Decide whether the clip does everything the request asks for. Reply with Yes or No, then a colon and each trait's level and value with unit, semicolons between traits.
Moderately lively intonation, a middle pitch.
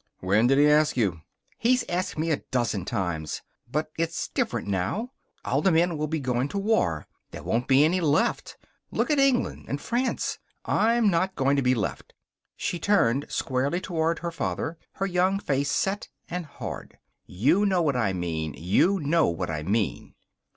No: wide, 7.7 semitones; medium, 150 Hz